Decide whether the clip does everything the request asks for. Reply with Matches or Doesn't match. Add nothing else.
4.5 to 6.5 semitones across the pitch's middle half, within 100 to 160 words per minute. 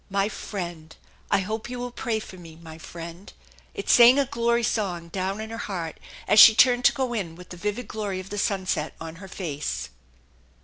Doesn't match